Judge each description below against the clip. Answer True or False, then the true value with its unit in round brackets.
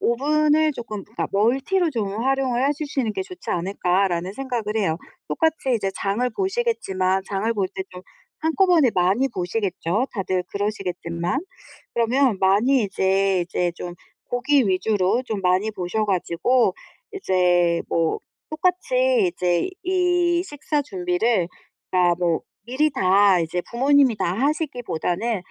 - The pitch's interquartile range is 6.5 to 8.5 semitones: True (7.2 semitones)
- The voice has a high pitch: True (220 Hz)